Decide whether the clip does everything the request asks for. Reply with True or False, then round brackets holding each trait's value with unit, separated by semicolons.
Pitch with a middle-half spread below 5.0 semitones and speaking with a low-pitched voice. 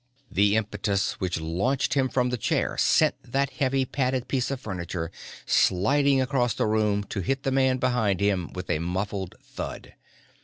False (5.3 semitones; 110 Hz)